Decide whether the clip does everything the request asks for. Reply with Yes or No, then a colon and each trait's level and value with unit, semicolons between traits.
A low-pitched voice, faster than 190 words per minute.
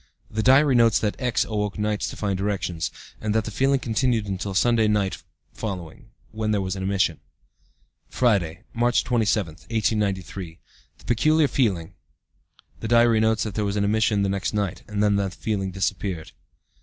No: low, 105 Hz; average, 170 wpm